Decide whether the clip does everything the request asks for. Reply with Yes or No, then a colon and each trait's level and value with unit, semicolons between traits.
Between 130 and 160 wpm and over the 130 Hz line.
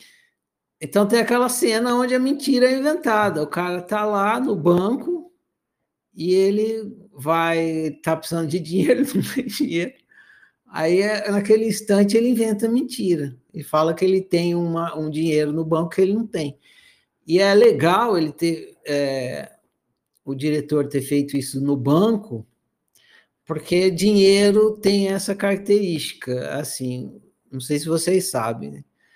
Yes: average, 150 wpm; medium, 185 Hz